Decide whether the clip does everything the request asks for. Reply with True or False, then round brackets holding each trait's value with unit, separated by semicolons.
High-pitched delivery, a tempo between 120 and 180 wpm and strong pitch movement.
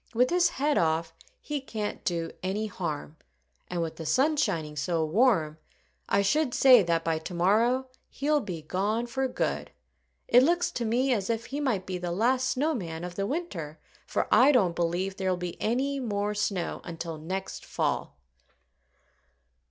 True (200 Hz; 170 wpm; 7.1 semitones)